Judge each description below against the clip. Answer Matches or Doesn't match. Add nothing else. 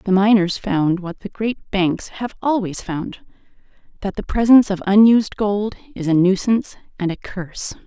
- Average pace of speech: Matches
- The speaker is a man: Doesn't match